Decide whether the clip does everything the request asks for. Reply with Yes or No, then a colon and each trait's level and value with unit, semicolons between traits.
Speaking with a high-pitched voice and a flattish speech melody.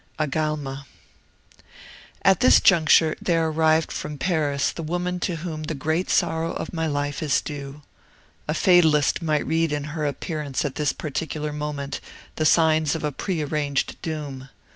No: medium, 155 Hz; narrow, 2.0 semitones